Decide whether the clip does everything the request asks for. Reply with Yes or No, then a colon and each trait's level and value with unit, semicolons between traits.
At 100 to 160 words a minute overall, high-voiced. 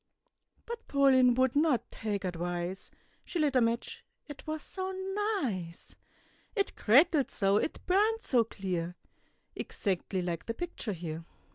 Yes: slow, 135 wpm; high, 230 Hz